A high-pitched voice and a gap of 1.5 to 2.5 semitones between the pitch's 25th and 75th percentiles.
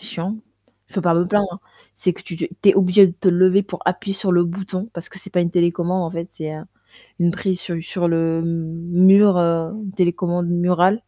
No: medium, 180 Hz; narrow, 2.0 semitones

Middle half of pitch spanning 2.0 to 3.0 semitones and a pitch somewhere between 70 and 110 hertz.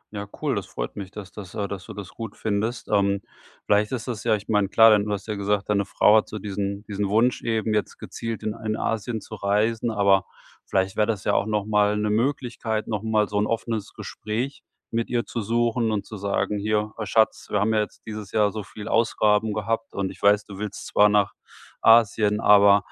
No: narrow, 1.6 semitones; low, 105 Hz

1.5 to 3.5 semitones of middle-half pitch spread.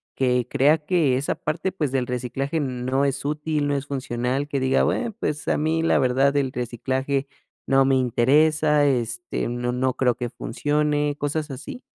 Yes: average, 2.9 semitones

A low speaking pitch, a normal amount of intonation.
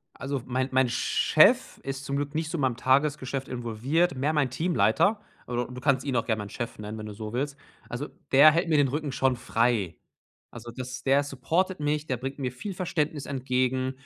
Yes: low, 130 Hz; average, 3.1 semitones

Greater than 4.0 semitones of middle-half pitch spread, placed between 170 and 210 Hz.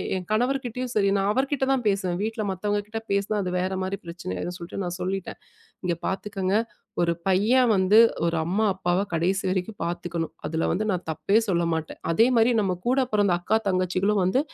No: average, 3.3 semitones; high, 190 Hz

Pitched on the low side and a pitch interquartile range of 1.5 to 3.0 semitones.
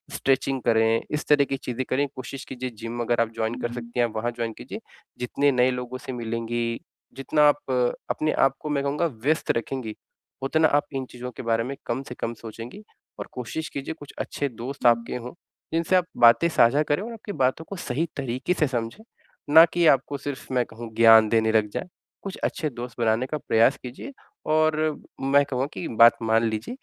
No: low, 125 Hz; average, 3.7 semitones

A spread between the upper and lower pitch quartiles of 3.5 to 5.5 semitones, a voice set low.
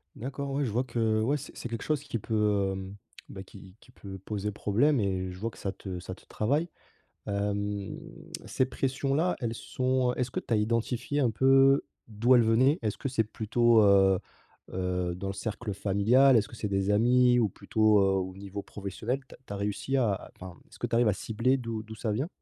Yes: average, 4.1 semitones; low, 110 Hz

